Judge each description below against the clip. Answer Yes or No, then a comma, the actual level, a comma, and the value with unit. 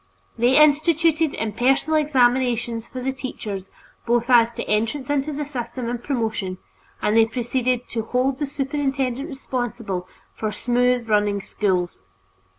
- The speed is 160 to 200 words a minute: No, slow, 135 wpm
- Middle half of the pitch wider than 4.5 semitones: No, average, 3.3 semitones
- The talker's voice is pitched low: No, high, 245 Hz